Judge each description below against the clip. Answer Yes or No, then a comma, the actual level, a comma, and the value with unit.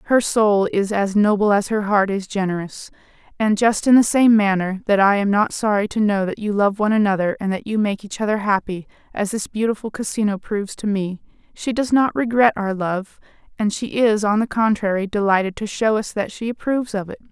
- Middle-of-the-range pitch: No, high, 210 Hz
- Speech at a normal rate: No, fast, 220 wpm